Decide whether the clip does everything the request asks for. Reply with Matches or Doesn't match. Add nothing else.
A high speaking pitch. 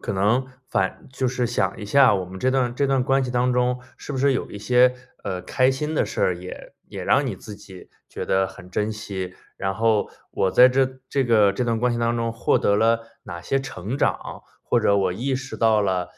Doesn't match